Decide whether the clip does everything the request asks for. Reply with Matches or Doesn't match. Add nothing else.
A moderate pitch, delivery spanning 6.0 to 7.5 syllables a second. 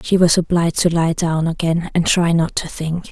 Doesn't match